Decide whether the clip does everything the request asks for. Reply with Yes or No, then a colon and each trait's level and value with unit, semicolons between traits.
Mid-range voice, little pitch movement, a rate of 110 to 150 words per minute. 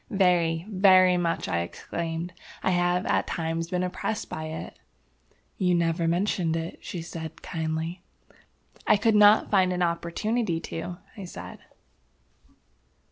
Yes: medium, 175 Hz; narrow, 2.1 semitones; slow, 135 wpm